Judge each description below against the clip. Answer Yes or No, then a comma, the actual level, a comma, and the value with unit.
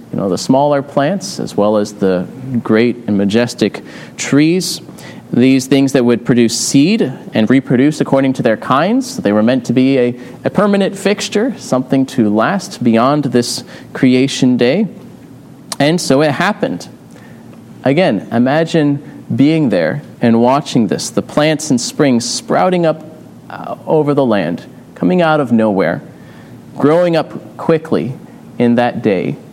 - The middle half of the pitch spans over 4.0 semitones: Yes, wide, 5.4 semitones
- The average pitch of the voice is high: No, medium, 140 Hz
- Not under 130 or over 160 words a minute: Yes, average, 145 wpm